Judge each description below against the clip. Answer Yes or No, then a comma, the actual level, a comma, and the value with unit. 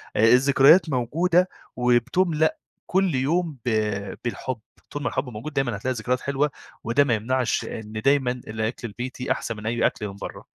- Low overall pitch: Yes, low, 130 Hz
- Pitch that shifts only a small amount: No, average, 3.6 semitones